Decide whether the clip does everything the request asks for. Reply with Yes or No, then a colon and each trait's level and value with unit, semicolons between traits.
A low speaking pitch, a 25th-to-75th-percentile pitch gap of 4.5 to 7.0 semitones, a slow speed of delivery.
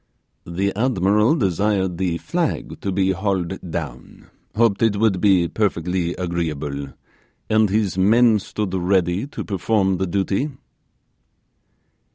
No: very low, 95 Hz; average, 3.2 semitones; slow, 120 wpm